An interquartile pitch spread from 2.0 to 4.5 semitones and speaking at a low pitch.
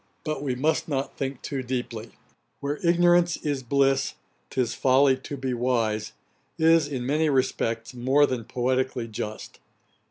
Yes: average, 2.9 semitones; low, 130 Hz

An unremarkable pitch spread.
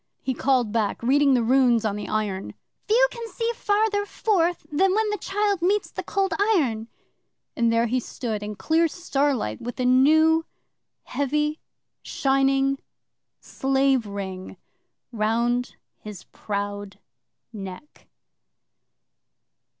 No: wide, 7.0 semitones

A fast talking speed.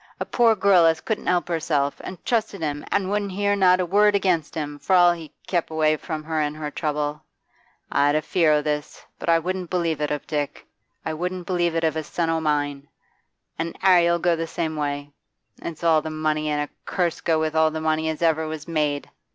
Yes: fast, 225 wpm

